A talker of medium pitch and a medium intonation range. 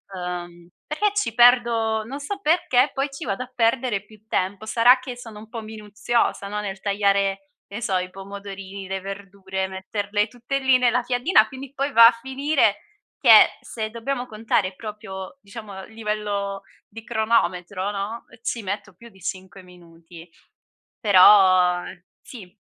No: high, 210 Hz; average, 3.6 semitones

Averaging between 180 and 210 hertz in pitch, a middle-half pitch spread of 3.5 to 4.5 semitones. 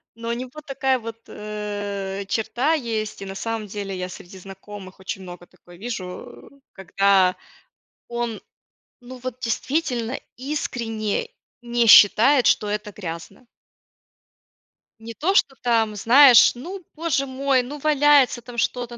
No: high, 230 Hz; average, 4.2 semitones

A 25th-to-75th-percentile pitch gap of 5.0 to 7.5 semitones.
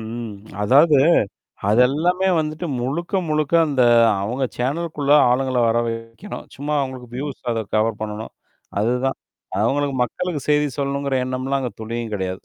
No: average, 4.0 semitones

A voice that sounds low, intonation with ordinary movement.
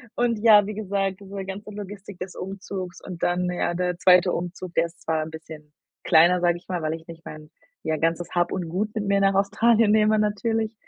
No: medium, 185 Hz; average, 3.0 semitones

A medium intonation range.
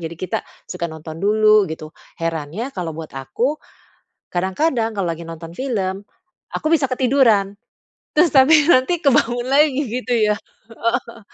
No: wide, 7.4 semitones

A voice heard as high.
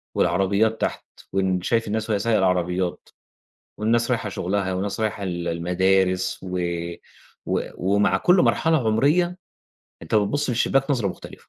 No: low, 100 Hz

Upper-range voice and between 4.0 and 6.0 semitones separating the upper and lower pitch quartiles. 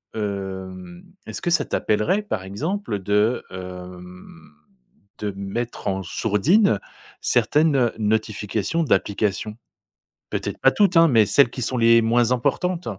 No: low, 110 Hz; wide, 5.5 semitones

